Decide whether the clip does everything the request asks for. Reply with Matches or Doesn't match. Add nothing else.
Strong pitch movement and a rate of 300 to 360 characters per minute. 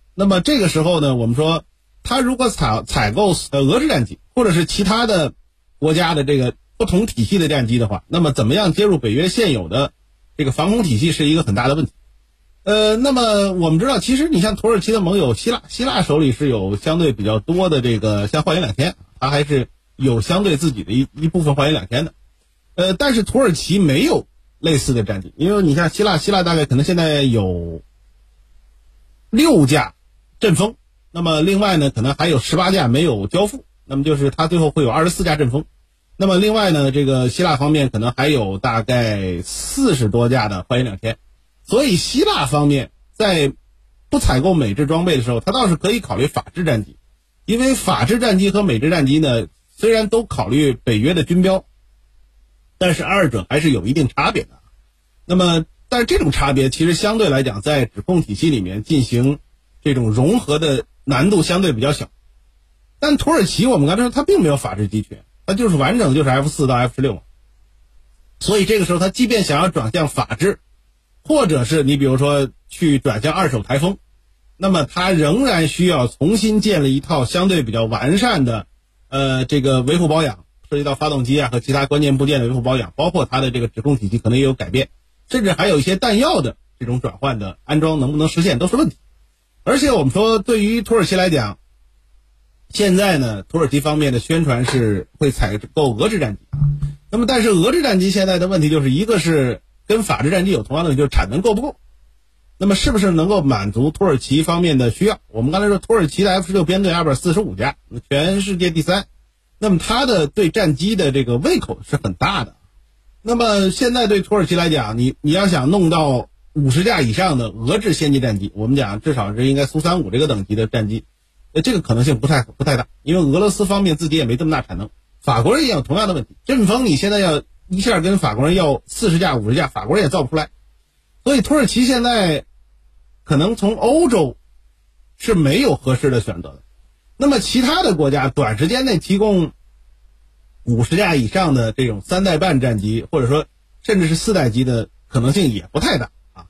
Matches